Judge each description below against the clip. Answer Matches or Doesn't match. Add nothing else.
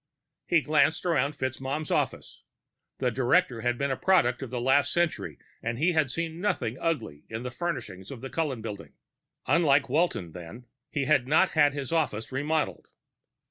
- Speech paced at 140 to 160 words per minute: Doesn't match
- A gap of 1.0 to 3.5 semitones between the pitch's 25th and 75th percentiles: Doesn't match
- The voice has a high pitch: Doesn't match